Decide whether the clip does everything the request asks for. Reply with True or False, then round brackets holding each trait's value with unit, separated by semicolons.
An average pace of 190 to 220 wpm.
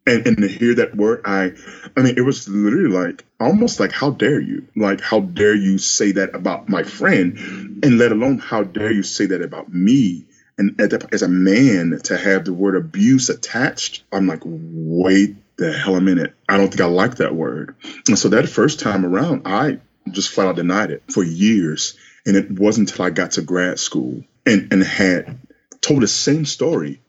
True (200 wpm)